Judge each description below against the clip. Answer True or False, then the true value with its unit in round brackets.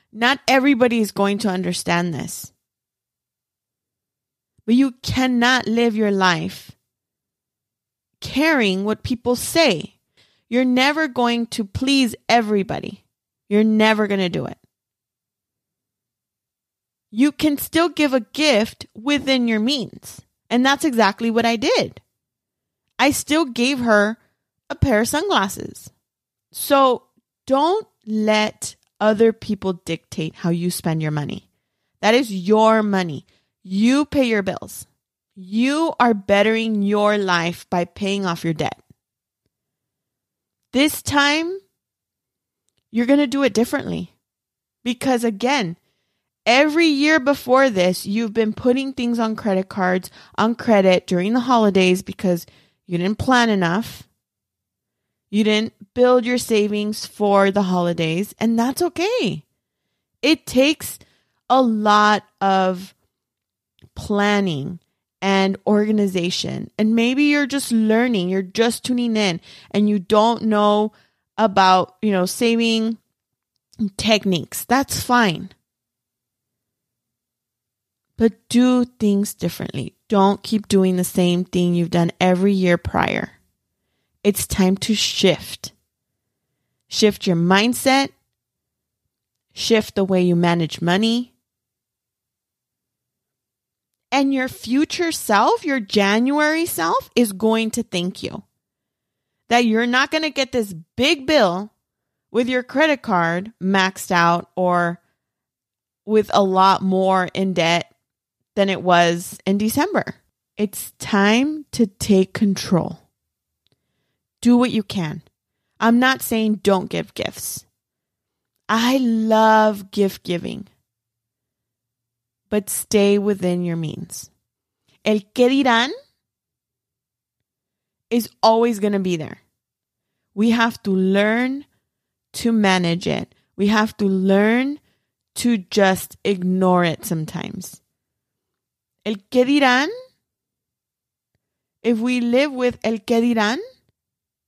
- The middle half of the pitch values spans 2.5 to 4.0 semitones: False (5.1 semitones)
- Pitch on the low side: False (210 Hz)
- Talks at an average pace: False (115 wpm)